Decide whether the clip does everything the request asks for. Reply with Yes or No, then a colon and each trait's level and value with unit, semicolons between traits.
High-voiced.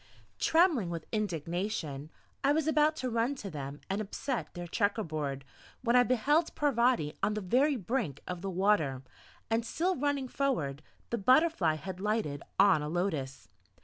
Yes: high, 210 Hz